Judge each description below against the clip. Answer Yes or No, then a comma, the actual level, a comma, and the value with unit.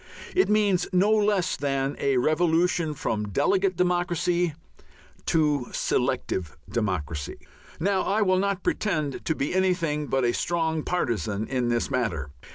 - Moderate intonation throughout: No, wide, 6.4 semitones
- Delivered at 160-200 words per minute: No, slow, 135 wpm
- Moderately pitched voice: Yes, medium, 160 Hz